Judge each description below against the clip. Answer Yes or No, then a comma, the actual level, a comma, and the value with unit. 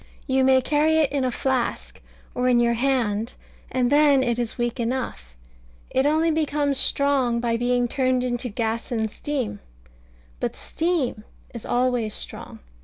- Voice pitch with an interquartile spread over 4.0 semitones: No, average, 2.9 semitones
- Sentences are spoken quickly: No, average, 155 wpm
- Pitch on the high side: Yes, very high, 255 Hz